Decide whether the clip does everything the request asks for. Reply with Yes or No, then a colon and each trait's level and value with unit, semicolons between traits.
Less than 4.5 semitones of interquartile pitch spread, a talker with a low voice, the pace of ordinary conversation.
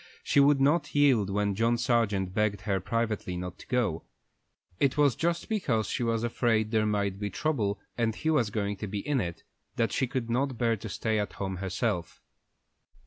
Yes: average, 4.1 semitones; low, 110 Hz; average, 195 wpm